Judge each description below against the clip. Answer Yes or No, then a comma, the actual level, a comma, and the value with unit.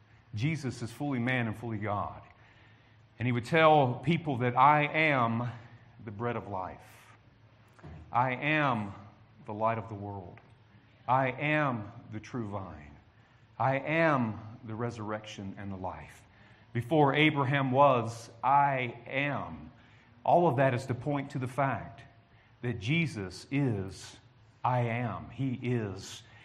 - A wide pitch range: No, average, 3.5 semitones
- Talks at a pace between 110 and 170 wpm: Yes, slow, 135 wpm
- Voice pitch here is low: Yes, low, 120 Hz